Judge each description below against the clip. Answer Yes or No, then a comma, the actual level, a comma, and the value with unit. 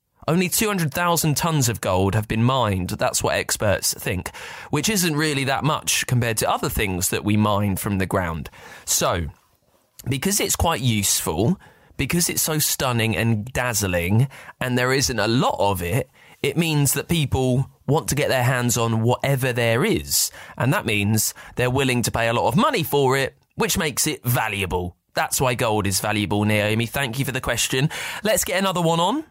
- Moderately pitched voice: No, low, 125 Hz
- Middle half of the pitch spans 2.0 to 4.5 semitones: No, average, 5.0 semitones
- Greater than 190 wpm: No, average, 185 wpm